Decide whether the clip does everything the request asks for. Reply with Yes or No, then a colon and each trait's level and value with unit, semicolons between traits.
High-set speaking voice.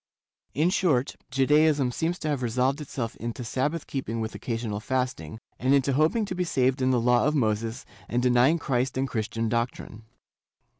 No: low, 130 Hz